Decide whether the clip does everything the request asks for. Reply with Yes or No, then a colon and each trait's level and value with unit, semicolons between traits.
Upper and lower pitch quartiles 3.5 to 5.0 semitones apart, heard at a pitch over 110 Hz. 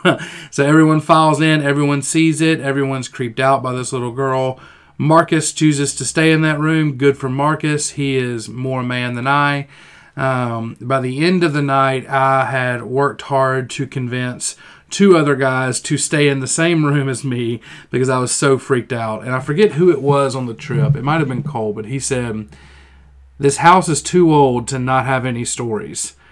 No: average, 3.1 semitones; low, 135 Hz